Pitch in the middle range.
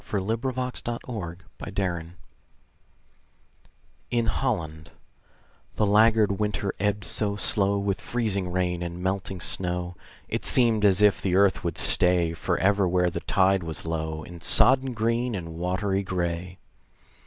No: very low, 95 Hz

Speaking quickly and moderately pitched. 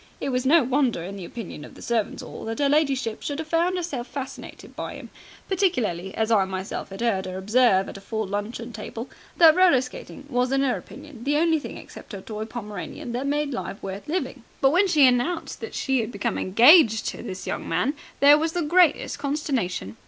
No: fast, 210 wpm; very high, 250 Hz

